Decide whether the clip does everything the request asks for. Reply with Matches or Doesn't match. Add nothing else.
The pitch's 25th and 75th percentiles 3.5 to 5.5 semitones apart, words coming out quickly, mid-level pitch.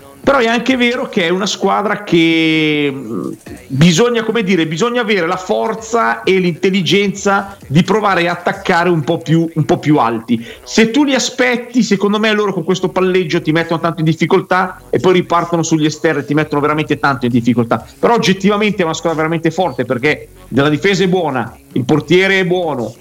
Matches